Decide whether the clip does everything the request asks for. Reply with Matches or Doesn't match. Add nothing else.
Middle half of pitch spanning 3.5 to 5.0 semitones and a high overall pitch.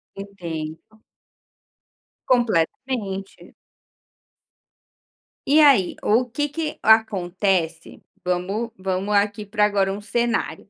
Matches